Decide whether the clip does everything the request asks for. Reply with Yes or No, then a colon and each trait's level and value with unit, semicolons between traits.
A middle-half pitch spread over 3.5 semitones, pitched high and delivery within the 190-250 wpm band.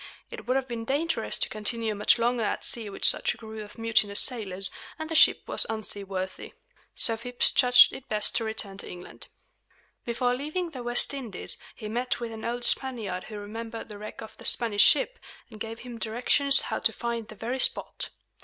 No: narrow, 2.6 semitones; high, 230 Hz; average, 200 wpm